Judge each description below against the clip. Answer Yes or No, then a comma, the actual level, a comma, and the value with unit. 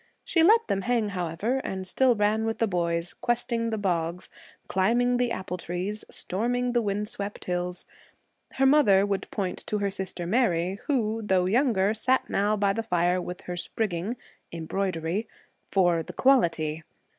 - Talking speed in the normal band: Yes, average, 160 wpm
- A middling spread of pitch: Yes, average, 4.4 semitones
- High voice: Yes, high, 200 Hz